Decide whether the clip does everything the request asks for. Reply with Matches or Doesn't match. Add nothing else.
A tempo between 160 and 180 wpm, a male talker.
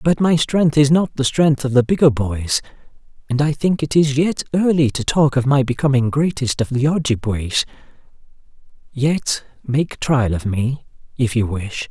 Matches